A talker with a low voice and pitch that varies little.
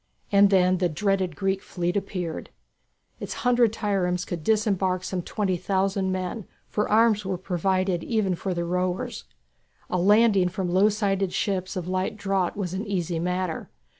No: high, 190 Hz; narrow, 2.0 semitones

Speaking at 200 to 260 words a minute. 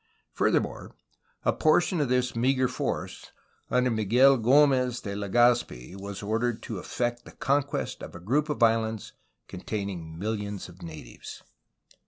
No: average, 140 wpm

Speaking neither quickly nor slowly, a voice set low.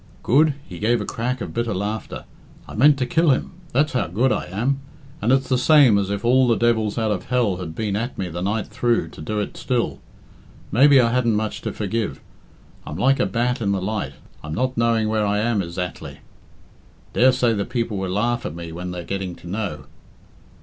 No: fast, 210 wpm; low, 110 Hz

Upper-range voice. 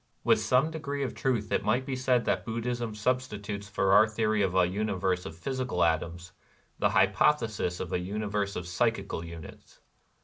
No: low, 105 Hz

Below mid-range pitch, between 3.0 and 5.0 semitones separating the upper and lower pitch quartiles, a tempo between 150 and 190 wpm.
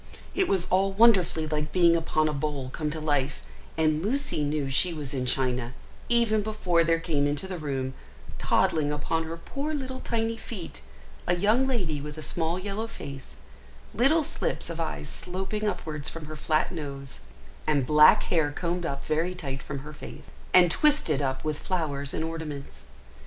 No: medium, 160 Hz; average, 4.6 semitones; average, 175 wpm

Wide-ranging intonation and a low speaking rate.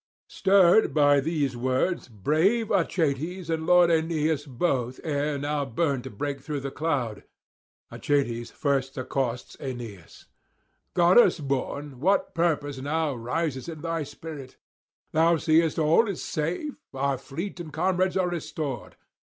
No: average, 3.9 semitones; slow, 130 wpm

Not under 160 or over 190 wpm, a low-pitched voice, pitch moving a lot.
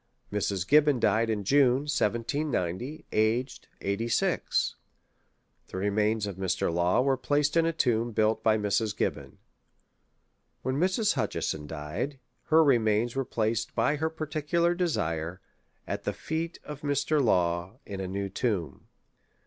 No: slow, 135 wpm; low, 115 Hz; wide, 6.4 semitones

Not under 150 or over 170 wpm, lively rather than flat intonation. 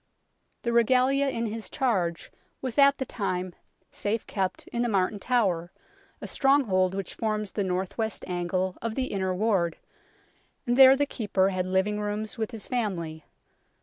No: average, 160 wpm; average, 4.3 semitones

